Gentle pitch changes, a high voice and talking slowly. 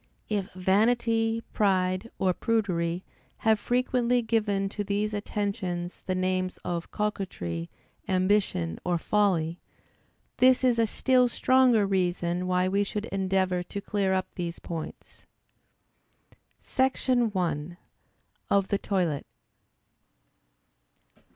No: average, 3.4 semitones; high, 195 Hz; slow, 105 wpm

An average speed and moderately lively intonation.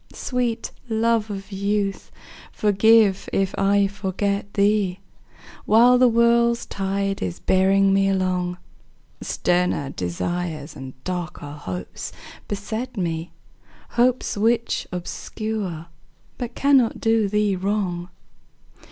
No: slow, 100 wpm; average, 3.6 semitones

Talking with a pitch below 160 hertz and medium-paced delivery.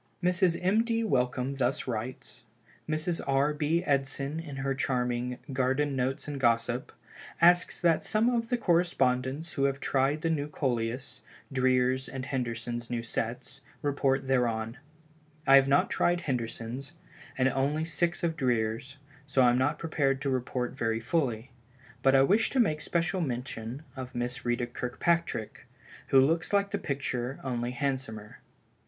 Yes: low, 135 Hz; average, 155 wpm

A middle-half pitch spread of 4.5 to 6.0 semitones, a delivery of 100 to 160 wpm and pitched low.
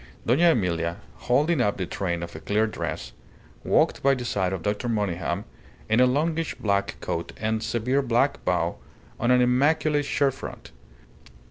Yes: wide, 5.5 semitones; average, 155 wpm; low, 115 Hz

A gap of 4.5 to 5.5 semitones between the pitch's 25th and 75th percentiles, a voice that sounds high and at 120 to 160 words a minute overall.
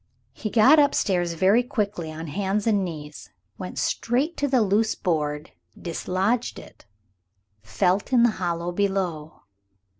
Yes: average, 5.0 semitones; high, 195 Hz; average, 140 wpm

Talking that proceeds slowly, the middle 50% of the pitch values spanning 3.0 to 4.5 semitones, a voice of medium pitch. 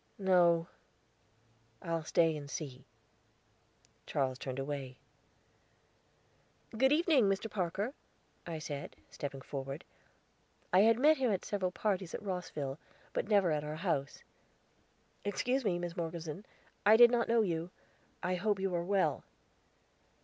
No: slow, 130 wpm; average, 5.3 semitones; medium, 180 Hz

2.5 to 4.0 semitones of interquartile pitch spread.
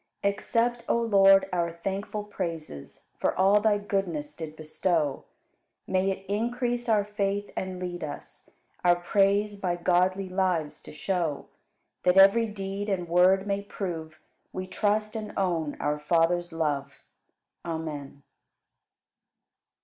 Yes: average, 3.4 semitones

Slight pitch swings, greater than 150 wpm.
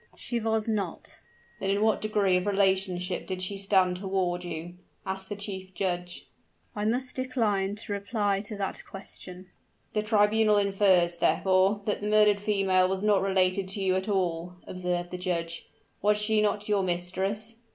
Yes: narrow, 2.2 semitones; average, 165 wpm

